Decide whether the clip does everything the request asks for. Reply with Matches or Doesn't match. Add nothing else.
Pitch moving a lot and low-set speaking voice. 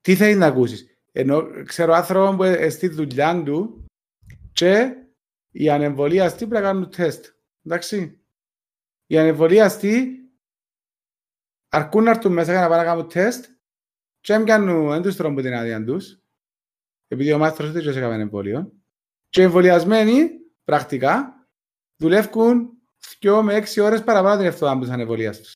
Doesn't match